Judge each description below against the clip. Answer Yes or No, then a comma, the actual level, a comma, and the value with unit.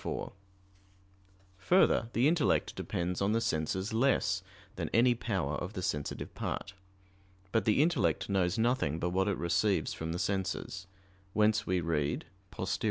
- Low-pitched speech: Yes, very low, 95 Hz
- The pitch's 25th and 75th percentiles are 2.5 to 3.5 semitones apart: No, average, 4.3 semitones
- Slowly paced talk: No, average, 150 wpm